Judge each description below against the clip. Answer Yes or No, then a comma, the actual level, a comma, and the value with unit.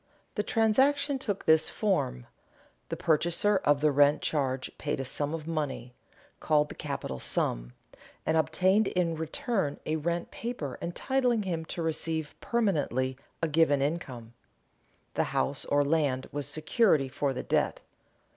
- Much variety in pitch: No, average, 4.5 semitones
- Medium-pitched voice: Yes, medium, 155 Hz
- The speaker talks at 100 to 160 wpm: Yes, average, 145 wpm